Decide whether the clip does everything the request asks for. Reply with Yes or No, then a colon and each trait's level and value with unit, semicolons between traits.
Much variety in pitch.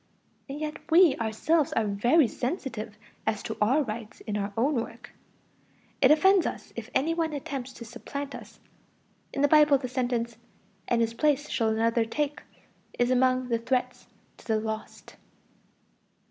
No: average, 4.3 semitones